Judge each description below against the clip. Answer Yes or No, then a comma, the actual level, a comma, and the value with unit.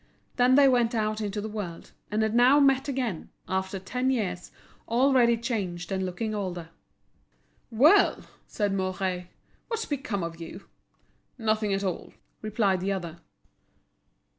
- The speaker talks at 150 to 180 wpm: No, average, 140 wpm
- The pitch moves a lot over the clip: No, average, 4.7 semitones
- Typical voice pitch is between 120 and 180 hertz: No, high, 215 Hz